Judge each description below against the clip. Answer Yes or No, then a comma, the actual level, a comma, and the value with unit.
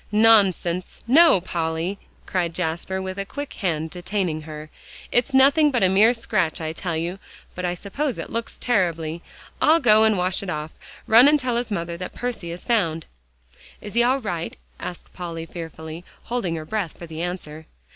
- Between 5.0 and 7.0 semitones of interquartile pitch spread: Yes, average, 5.3 semitones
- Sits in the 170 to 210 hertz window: Yes, medium, 185 Hz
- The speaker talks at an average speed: Yes, average, 180 wpm